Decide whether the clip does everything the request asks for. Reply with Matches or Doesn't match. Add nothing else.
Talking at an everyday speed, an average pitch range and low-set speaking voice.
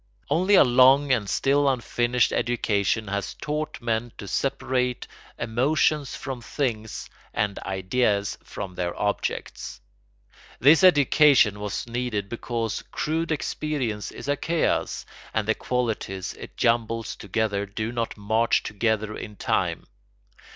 Doesn't match